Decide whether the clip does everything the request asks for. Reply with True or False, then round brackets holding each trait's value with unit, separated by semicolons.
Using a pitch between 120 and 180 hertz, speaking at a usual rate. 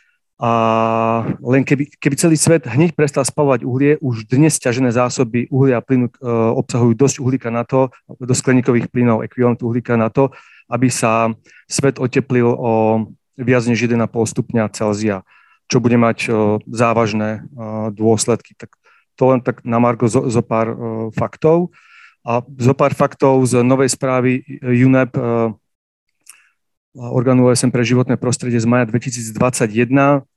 True (125 Hz; 145 wpm)